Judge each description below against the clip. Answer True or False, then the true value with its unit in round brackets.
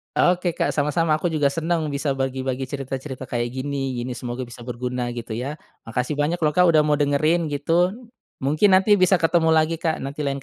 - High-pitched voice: False (145 Hz)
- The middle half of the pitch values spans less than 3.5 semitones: False (3.8 semitones)